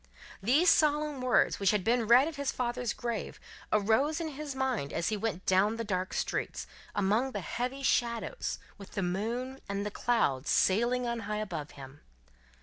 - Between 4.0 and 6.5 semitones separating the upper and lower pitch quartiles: Yes, average, 4.6 semitones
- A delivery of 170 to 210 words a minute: Yes, average, 175 wpm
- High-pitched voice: Yes, high, 230 Hz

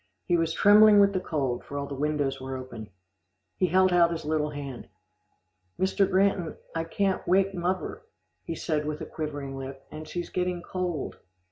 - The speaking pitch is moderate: Yes, medium, 165 Hz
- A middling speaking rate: Yes, average, 170 wpm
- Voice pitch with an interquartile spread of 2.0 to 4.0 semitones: No, average, 4.5 semitones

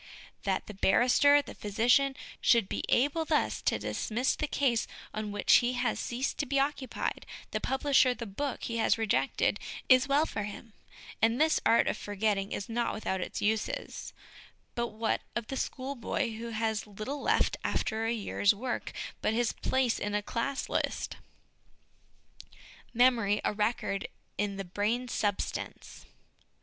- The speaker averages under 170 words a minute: Yes, average, 160 wpm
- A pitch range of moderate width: Yes, average, 3.8 semitones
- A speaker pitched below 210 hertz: No, high, 230 Hz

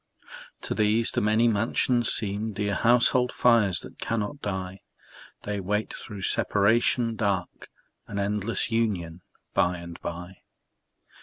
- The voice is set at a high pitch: No, low, 105 Hz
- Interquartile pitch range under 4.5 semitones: Yes, average, 3.1 semitones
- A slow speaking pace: Yes, slow, 125 wpm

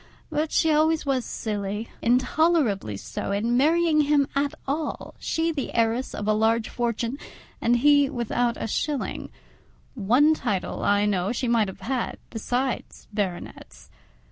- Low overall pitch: No, high, 245 Hz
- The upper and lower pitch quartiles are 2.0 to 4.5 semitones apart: No, wide, 5.4 semitones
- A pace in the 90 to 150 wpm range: Yes, average, 140 wpm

